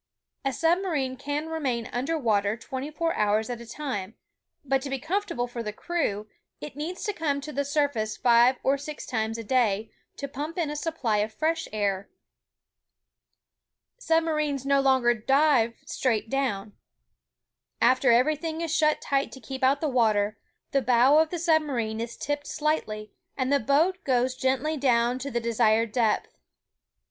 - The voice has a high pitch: Yes, very high, 265 Hz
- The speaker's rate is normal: Yes, average, 170 wpm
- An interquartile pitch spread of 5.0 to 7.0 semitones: No, average, 4.6 semitones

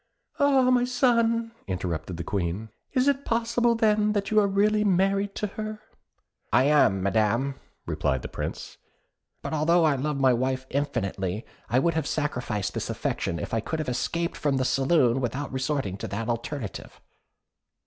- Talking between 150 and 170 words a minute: Yes, average, 165 wpm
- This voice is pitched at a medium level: Yes, medium, 145 Hz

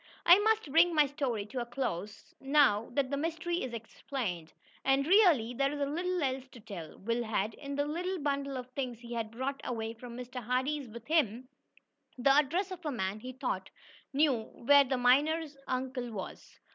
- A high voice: Yes, very high, 265 Hz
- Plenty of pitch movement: No, average, 4.0 semitones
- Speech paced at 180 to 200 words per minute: Yes, average, 185 wpm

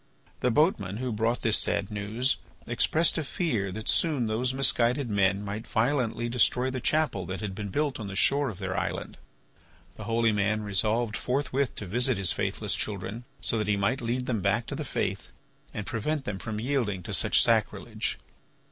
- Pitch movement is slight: No, average, 4.0 semitones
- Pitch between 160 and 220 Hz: No, low, 115 Hz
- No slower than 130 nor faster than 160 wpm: No, average, 185 wpm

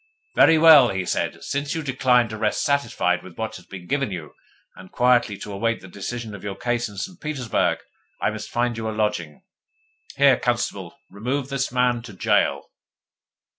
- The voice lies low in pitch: Yes, low, 115 Hz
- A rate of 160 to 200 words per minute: Yes, average, 180 wpm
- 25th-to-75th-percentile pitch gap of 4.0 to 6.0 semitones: Yes, average, 4.5 semitones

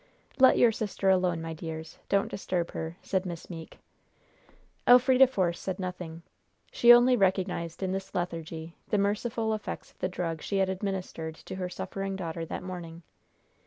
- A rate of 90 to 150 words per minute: No, average, 160 wpm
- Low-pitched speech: No, medium, 185 Hz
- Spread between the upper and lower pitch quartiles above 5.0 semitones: No, average, 3.1 semitones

